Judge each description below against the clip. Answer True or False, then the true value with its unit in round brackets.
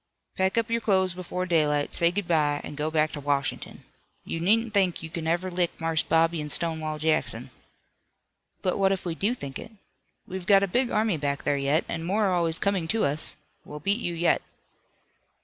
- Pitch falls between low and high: True (170 Hz)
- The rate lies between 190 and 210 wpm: True (200 wpm)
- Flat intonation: False (3.7 semitones)